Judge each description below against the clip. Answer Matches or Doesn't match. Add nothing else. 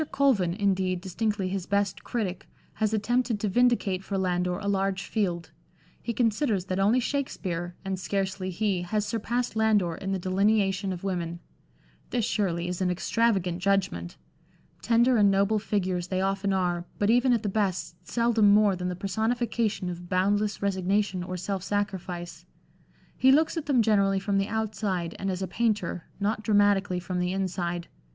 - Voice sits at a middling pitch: Doesn't match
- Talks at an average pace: Matches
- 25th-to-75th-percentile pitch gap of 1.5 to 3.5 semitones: Matches